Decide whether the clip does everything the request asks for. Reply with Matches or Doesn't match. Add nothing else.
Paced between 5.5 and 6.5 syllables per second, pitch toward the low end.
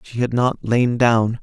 Doesn't match